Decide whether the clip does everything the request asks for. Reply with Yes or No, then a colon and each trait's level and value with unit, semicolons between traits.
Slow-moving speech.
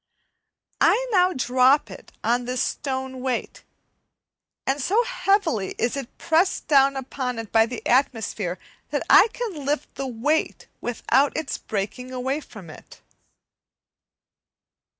Yes: slow, 130 wpm